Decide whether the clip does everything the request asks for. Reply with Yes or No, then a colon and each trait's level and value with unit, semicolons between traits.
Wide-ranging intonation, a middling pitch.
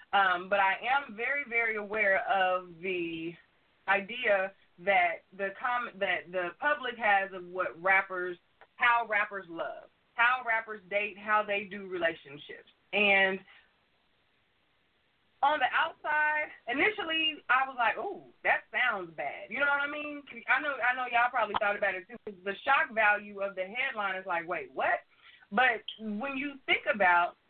No: wide, 5.8 semitones; high, 215 Hz